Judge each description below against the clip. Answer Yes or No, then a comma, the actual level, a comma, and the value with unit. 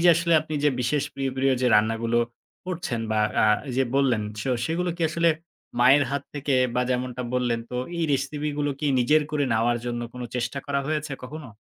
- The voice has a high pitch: No, low, 135 Hz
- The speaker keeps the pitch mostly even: No, average, 3.7 semitones